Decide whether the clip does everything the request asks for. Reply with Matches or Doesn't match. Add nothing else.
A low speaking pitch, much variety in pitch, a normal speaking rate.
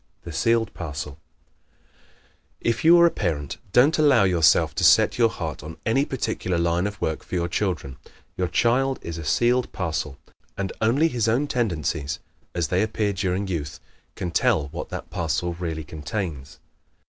Matches